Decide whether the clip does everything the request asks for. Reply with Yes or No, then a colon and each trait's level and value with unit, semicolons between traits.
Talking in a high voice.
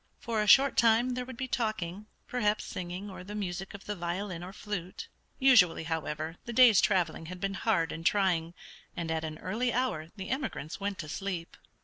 Yes: high, 195 Hz